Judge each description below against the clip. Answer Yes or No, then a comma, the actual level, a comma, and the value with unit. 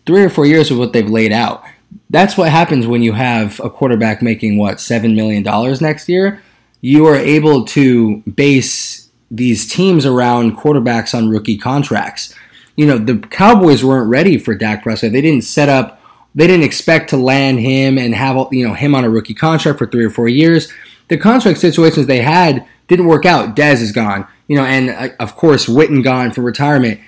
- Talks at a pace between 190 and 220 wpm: Yes, average, 200 wpm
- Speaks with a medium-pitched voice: No, low, 130 Hz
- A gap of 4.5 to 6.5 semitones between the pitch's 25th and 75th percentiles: Yes, average, 4.8 semitones